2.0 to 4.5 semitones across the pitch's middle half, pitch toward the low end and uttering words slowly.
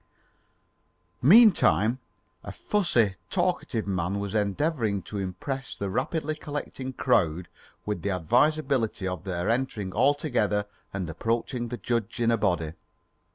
No: wide, 5.5 semitones; low, 115 Hz; slow, 125 wpm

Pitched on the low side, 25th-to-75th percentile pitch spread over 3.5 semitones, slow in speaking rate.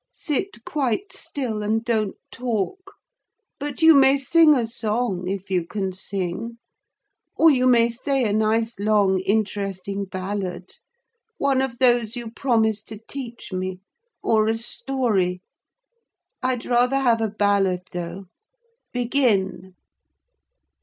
No: high, 225 Hz; average, 4.5 semitones; slow, 120 wpm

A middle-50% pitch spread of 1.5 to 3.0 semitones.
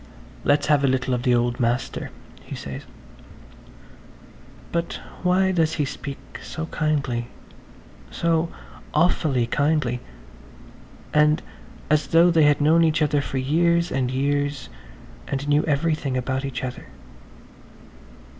No: average, 3.7 semitones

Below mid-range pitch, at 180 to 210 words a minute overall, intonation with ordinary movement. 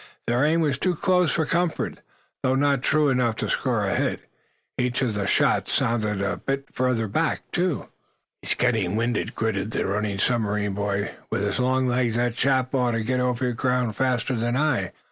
Yes: low, 125 Hz; average, 185 wpm; average, 3.6 semitones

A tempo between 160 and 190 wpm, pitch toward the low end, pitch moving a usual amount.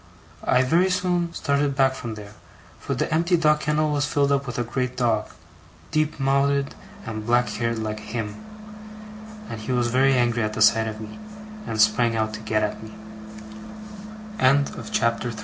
No: average, 150 wpm; low, 125 Hz; average, 4.3 semitones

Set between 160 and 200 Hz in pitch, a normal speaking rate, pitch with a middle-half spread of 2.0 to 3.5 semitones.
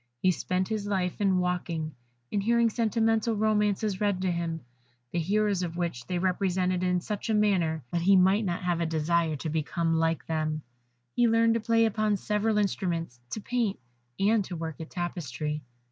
No: medium, 185 Hz; average, 180 wpm; average, 3.9 semitones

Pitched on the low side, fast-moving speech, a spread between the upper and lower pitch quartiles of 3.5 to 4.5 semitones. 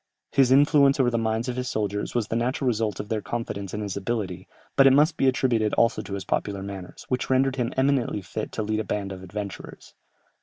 Yes: low, 115 Hz; fast, 225 wpm; average, 4.1 semitones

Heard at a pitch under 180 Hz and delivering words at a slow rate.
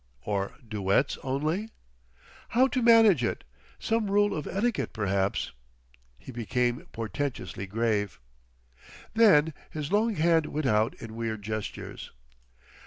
Yes: low, 135 Hz; slow, 115 wpm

